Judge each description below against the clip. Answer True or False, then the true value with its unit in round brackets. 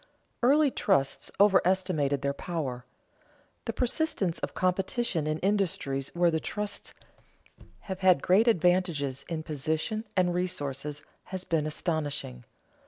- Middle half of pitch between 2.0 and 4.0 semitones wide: False (4.5 semitones)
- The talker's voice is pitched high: False (175 Hz)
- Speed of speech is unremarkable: False (120 wpm)